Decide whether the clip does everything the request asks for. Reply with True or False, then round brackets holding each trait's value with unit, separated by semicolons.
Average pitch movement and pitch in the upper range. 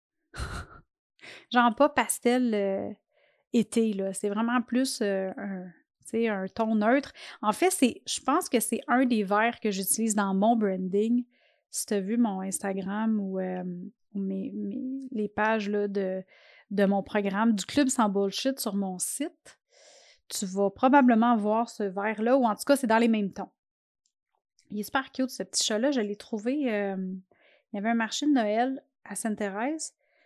True (4.1 semitones; 220 Hz)